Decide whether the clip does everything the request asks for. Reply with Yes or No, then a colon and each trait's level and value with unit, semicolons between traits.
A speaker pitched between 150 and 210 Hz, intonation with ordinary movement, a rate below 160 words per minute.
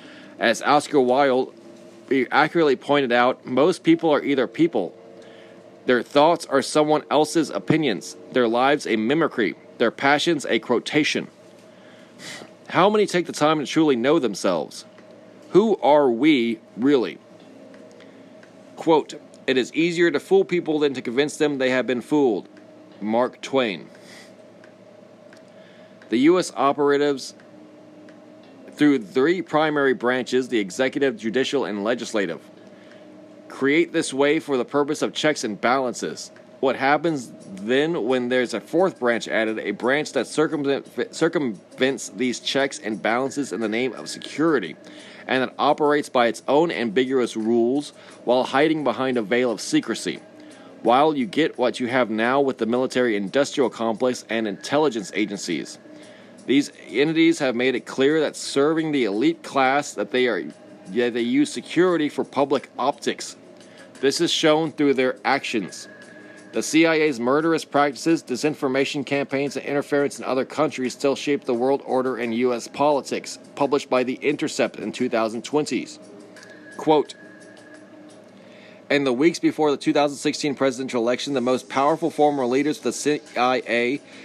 No: medium, 140 Hz; average, 3.4 semitones; average, 140 wpm